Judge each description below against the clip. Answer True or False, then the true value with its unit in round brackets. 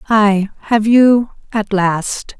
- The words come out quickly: False (125 wpm)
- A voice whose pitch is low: False (210 Hz)